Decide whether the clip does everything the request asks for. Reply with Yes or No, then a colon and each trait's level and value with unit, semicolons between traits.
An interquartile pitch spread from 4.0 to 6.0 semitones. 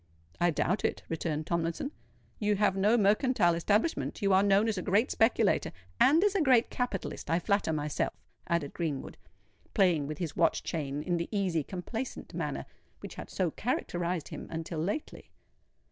Yes: average, 4.4 semitones